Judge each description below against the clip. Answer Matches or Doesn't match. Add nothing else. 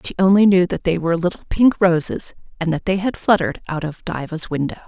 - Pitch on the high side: Doesn't match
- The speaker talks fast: Matches